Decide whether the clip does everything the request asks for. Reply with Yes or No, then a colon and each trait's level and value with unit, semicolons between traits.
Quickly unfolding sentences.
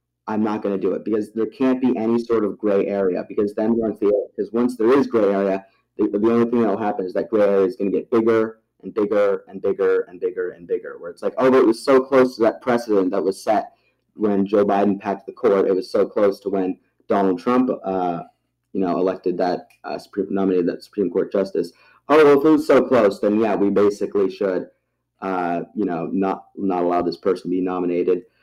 Yes: fast, 240 wpm